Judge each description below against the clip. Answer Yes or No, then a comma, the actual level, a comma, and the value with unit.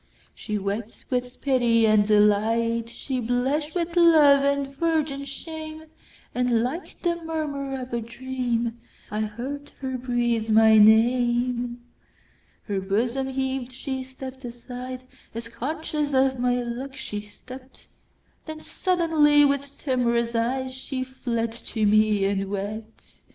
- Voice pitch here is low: No, very high, 250 Hz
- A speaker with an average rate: No, slow, 110 wpm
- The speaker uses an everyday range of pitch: Yes, average, 3.3 semitones